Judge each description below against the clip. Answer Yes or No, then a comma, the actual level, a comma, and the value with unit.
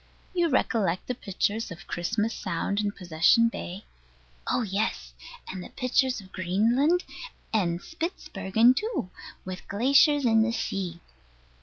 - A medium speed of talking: No, slow, 125 wpm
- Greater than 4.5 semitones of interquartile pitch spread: Yes, average, 5.2 semitones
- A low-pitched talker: No, high, 215 Hz